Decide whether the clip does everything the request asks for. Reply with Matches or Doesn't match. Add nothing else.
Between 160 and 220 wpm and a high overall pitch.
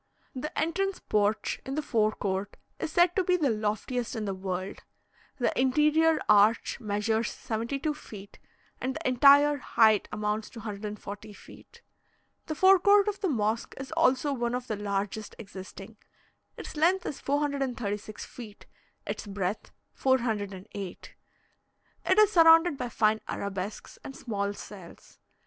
Doesn't match